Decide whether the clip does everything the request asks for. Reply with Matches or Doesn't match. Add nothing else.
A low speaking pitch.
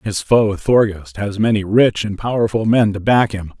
Matches